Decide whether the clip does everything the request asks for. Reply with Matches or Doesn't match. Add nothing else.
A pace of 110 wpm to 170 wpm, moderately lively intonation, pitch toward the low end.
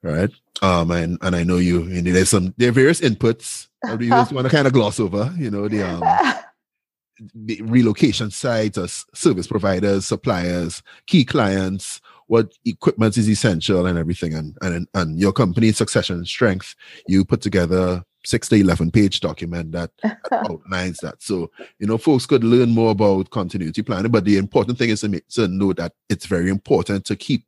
Doesn't match